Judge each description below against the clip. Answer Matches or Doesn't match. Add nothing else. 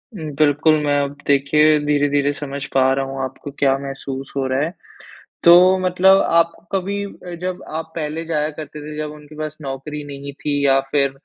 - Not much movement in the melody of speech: Matches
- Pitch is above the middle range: Doesn't match